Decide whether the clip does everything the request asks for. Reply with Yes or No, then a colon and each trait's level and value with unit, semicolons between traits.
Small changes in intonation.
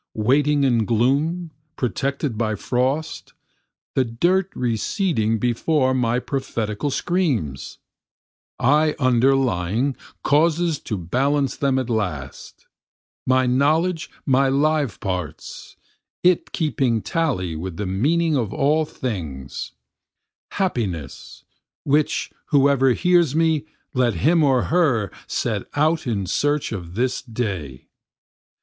No: wide, 5.4 semitones